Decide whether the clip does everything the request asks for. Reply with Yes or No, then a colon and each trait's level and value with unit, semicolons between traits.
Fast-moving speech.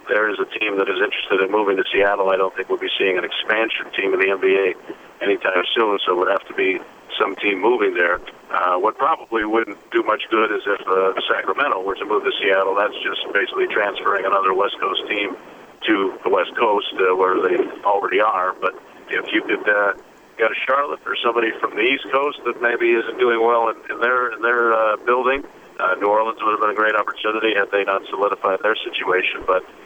Yes: fast, 220 wpm